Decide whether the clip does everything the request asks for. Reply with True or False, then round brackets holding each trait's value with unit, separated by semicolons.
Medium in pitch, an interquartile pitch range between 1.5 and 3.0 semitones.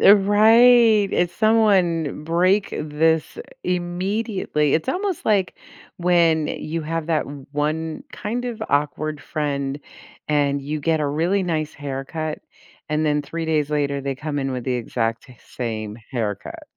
False (155 Hz; 4.4 semitones)